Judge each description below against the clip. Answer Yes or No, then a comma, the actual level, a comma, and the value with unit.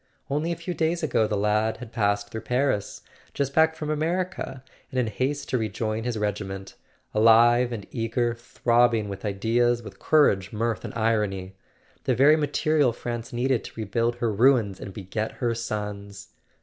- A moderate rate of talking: Yes, average, 170 wpm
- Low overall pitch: Yes, low, 115 Hz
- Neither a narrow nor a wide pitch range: Yes, average, 3.8 semitones